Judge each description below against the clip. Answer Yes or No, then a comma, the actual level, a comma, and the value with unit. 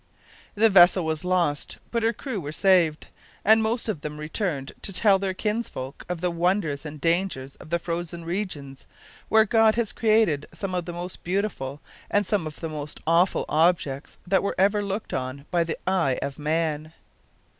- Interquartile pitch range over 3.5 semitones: Yes, average, 4.7 semitones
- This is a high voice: No, medium, 175 Hz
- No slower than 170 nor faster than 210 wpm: Yes, average, 185 wpm